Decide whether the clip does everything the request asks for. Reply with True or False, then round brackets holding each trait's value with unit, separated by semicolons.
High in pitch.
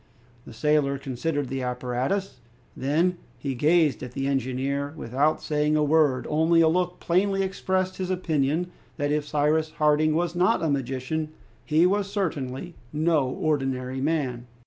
False (150 Hz)